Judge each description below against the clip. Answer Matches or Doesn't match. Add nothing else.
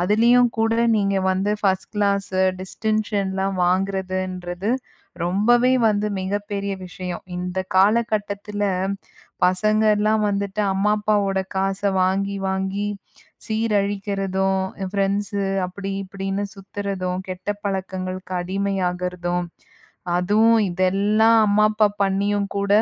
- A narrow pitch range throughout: Matches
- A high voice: Matches